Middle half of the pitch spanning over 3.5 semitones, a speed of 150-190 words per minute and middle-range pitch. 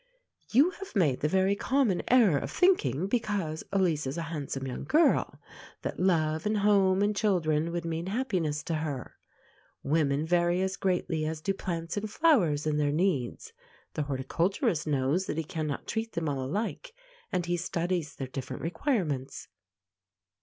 Yes: average, 4.8 semitones; average, 160 wpm; medium, 170 Hz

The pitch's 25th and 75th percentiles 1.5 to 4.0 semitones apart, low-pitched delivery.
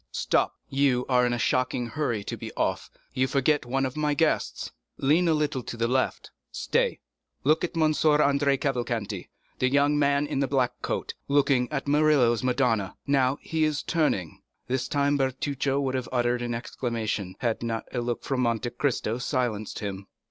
Yes: average, 2.9 semitones; low, 130 Hz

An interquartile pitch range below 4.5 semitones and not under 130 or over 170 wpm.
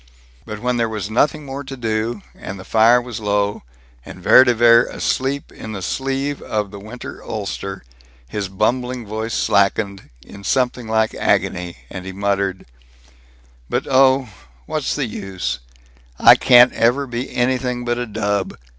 Yes: average, 3.7 semitones; average, 155 wpm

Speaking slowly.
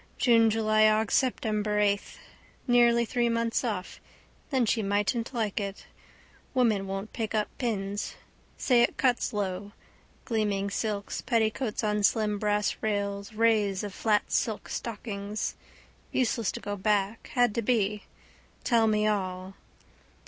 Yes: slow, 125 wpm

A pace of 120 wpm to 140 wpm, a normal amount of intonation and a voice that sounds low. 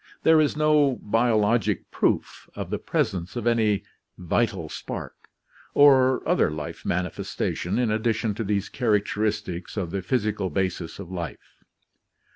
Yes: slow, 135 wpm; average, 4.5 semitones; low, 105 Hz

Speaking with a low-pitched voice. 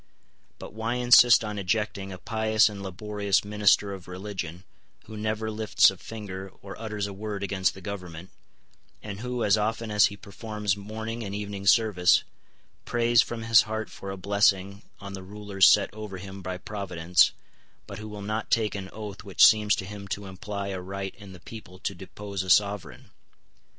Yes: low, 100 Hz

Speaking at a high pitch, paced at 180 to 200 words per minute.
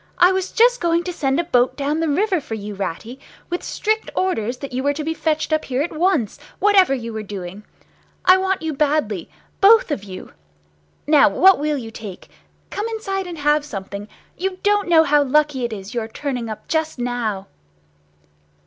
Yes: very high, 295 Hz; average, 190 wpm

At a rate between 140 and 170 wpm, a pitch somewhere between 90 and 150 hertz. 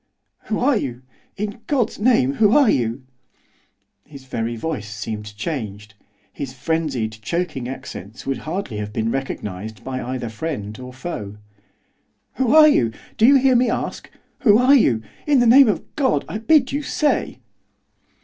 Yes: average, 160 wpm; medium, 140 Hz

